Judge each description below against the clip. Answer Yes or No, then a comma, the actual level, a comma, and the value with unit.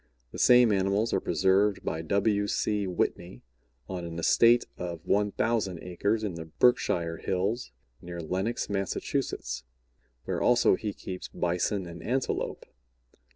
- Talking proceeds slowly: Yes, slow, 130 wpm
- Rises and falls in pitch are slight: No, average, 3.7 semitones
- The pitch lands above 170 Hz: No, very low, 95 Hz